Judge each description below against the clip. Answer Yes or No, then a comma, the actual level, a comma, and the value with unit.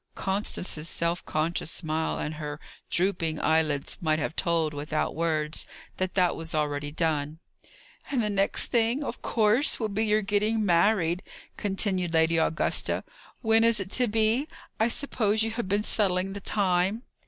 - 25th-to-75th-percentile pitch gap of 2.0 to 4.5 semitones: No, average, 5.0 semitones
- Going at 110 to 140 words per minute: No, average, 155 wpm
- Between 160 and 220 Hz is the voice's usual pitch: Yes, medium, 185 Hz